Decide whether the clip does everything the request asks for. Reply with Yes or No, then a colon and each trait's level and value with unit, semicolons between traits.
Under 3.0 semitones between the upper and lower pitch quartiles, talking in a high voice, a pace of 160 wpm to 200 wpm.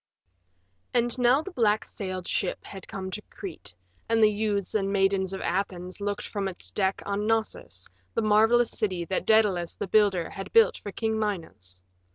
Yes: narrow, 2.6 semitones; high, 200 Hz; average, 180 wpm